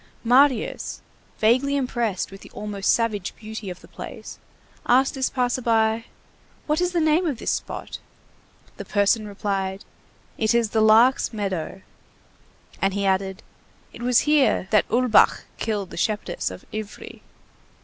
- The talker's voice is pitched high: Yes, high, 220 Hz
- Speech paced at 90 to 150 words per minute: Yes, average, 140 wpm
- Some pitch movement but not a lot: Yes, average, 3.9 semitones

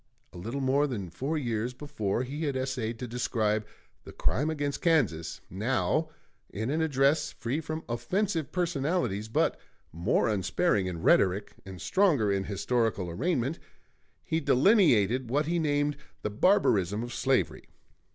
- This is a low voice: Yes, low, 125 Hz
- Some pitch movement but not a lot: No, wide, 6.0 semitones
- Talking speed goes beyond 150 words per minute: No, average, 140 wpm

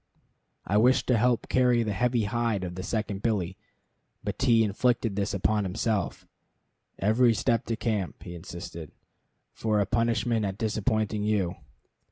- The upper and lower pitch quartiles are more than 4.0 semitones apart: No, average, 2.9 semitones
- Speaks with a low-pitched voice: Yes, low, 110 Hz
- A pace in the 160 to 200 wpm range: No, average, 145 wpm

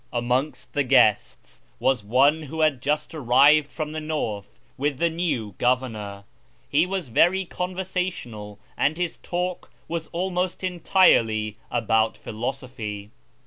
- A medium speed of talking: No, slow, 130 wpm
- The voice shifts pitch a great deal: Yes, wide, 6.7 semitones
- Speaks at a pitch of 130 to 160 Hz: Yes, medium, 140 Hz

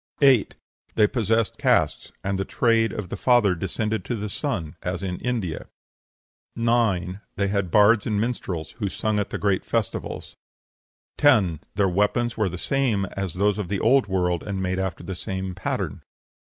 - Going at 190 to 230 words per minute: No, average, 170 wpm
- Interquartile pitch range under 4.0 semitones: Yes, average, 3.3 semitones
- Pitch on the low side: Yes, low, 100 Hz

